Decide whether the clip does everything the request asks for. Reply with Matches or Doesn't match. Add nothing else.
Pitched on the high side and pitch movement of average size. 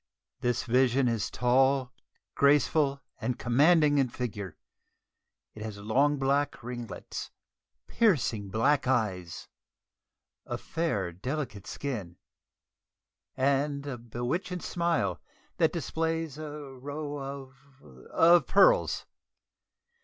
Doesn't match